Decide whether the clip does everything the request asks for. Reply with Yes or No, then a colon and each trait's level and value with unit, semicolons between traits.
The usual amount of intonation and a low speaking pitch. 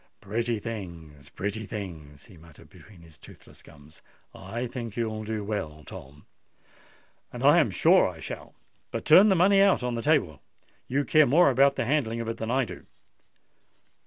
No: wide, 7.4 semitones; low, 110 Hz